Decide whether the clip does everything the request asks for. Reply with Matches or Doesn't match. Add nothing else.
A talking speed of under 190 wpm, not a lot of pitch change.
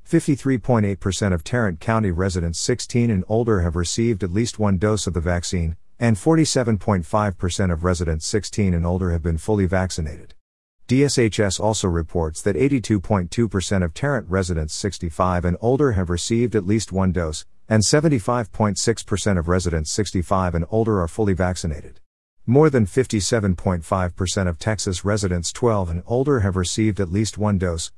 Doesn't match